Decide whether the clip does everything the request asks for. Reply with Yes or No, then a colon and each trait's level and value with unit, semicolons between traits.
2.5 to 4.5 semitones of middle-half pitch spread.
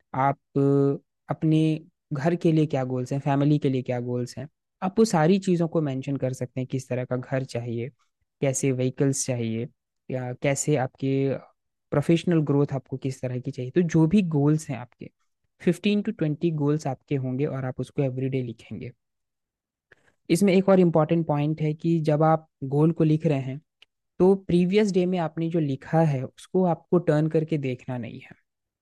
Yes: average, 3.9 semitones